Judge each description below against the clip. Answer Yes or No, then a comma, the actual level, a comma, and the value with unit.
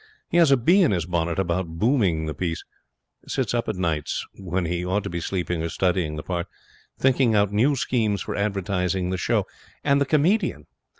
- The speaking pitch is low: Yes, very low, 95 Hz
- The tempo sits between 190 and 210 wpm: Yes, average, 195 wpm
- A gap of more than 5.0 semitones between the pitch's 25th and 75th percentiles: Yes, wide, 5.5 semitones